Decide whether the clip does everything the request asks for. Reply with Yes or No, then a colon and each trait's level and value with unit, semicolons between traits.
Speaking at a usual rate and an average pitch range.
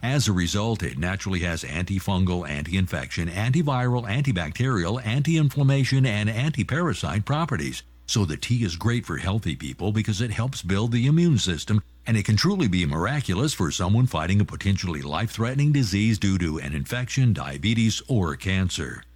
No: average, 165 wpm; wide, 5.9 semitones